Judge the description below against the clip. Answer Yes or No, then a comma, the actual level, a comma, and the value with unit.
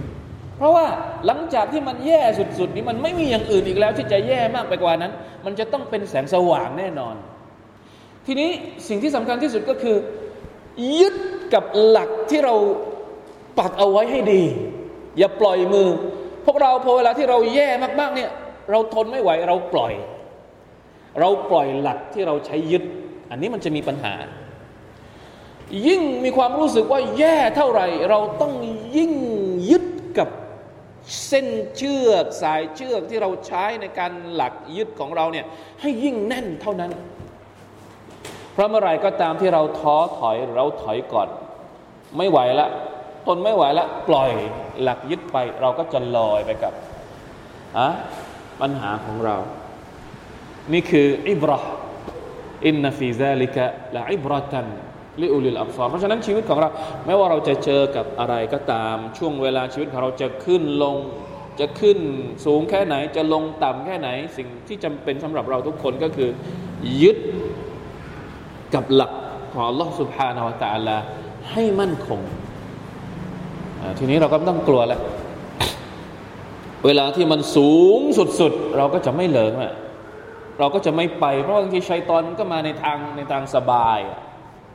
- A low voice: No, medium, 175 Hz